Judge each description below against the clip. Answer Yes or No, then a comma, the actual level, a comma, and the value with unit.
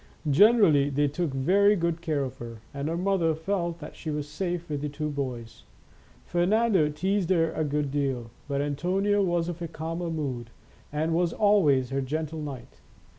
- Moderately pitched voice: Yes, medium, 155 Hz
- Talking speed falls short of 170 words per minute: No, average, 175 wpm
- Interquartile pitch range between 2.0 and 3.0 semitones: No, average, 3.8 semitones